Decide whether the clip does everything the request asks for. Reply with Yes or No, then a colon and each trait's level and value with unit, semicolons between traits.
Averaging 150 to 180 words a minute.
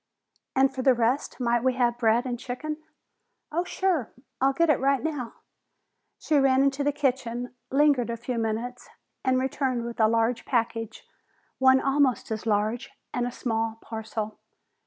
Yes: average, 160 wpm